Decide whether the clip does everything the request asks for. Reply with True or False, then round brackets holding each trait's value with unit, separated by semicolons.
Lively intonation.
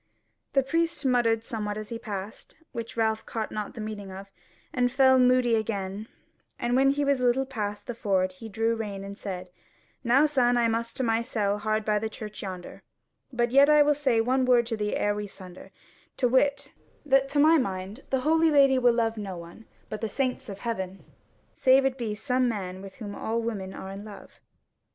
False (3.9 semitones)